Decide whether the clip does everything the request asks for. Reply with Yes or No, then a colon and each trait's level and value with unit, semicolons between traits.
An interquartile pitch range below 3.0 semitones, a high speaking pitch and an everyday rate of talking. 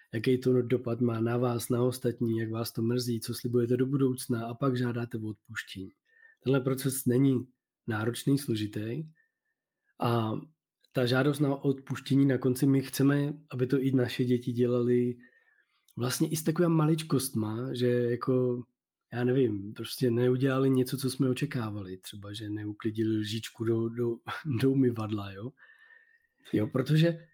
No: narrow, 2.5 semitones; low, 125 Hz; average, 145 wpm